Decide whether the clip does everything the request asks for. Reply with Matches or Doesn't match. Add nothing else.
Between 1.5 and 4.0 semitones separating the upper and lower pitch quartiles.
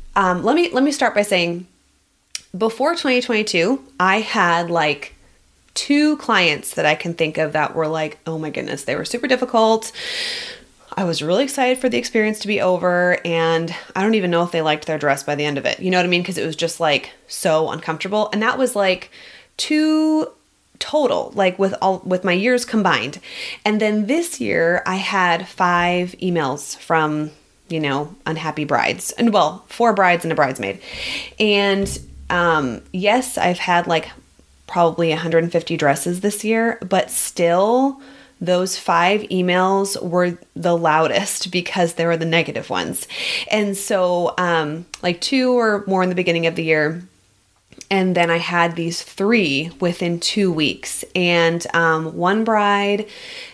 Doesn't match